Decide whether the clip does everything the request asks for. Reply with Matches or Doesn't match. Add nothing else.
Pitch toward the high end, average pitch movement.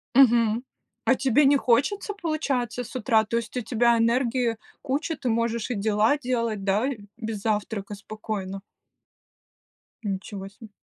Matches